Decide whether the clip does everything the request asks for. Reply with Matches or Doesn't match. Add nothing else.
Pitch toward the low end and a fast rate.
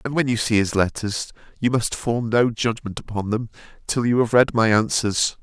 Matches